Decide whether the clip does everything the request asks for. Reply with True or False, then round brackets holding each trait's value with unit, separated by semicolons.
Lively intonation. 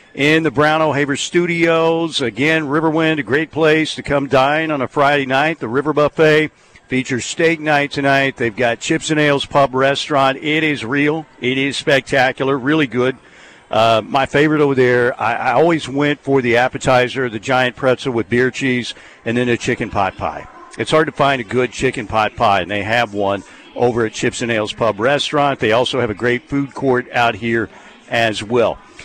False (3.6 semitones)